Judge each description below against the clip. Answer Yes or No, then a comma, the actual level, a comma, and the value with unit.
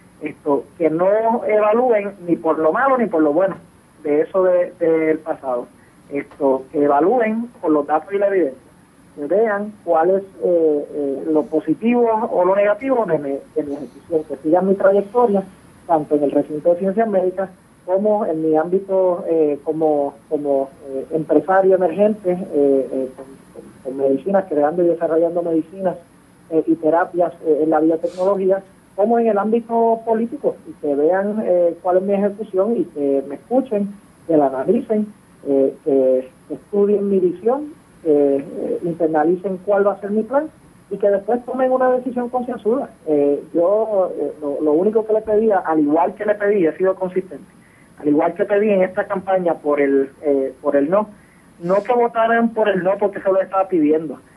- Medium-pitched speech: Yes, medium, 180 Hz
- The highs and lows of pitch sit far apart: No, average, 5.0 semitones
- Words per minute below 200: Yes, average, 175 wpm